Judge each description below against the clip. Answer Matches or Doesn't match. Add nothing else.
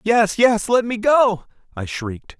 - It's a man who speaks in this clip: Matches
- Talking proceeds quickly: Doesn't match